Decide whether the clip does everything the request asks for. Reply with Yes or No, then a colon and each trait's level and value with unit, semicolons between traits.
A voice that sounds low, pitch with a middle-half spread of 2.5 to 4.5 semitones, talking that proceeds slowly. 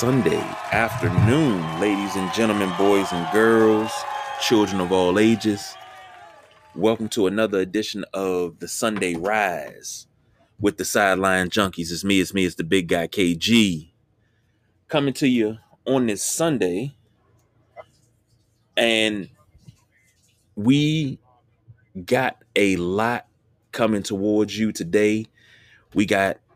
Yes: low, 110 Hz; average, 2.8 semitones; slow, 115 wpm